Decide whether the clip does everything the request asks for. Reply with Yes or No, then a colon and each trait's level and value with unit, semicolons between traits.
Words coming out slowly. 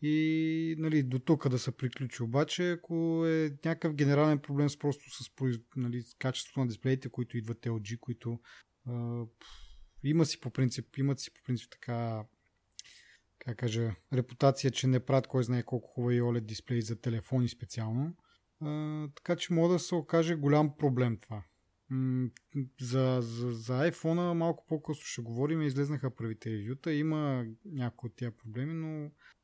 No: fast, 165 wpm